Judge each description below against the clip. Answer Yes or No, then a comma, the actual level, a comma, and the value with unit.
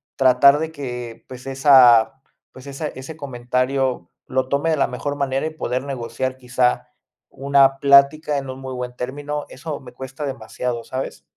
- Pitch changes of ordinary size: No, narrow, 1.9 semitones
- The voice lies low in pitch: Yes, low, 130 Hz